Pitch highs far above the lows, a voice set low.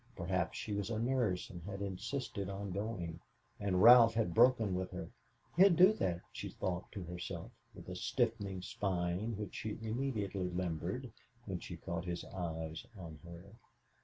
No: average, 4.3 semitones; low, 100 Hz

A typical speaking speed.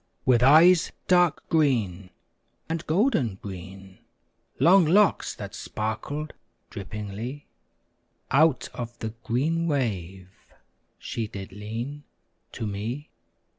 No: slow, 95 wpm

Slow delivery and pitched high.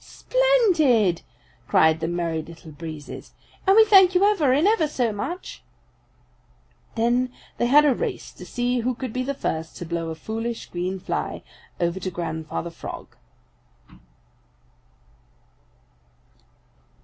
Yes: slow, 130 wpm; high, 230 Hz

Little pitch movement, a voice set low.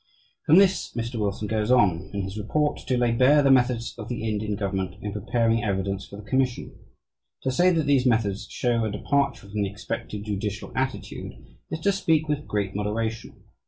No: average, 4.3 semitones; low, 115 Hz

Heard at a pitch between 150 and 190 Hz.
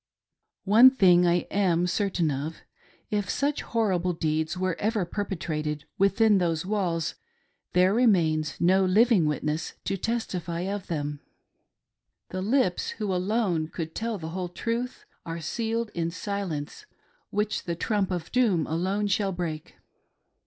Yes: medium, 185 Hz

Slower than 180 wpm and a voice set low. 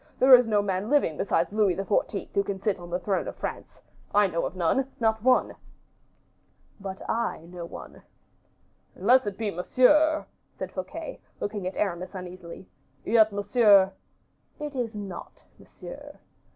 No: average, 155 wpm; high, 205 Hz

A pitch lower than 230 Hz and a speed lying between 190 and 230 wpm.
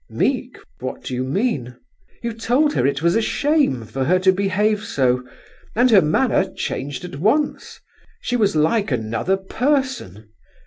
No: high, 190 Hz; average, 155 wpm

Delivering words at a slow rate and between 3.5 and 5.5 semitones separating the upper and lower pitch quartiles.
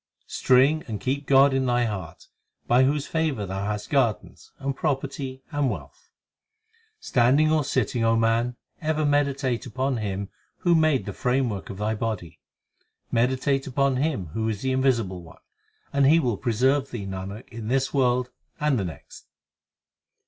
No: average, 155 wpm; average, 3.9 semitones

